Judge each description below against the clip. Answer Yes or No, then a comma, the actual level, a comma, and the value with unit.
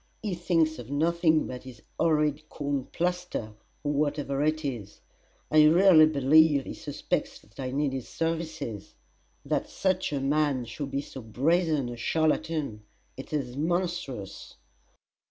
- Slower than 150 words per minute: Yes, average, 140 wpm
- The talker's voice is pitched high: No, medium, 150 Hz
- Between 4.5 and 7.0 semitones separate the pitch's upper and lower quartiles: No, average, 3.4 semitones